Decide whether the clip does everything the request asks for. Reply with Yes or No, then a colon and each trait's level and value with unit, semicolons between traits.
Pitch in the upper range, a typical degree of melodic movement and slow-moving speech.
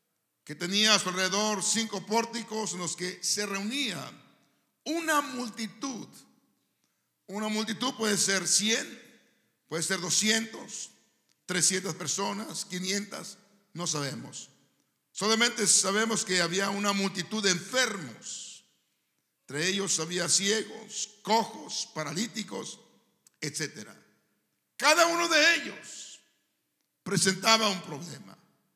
Yes: high, 205 Hz; average, 3.3 semitones; slow, 100 wpm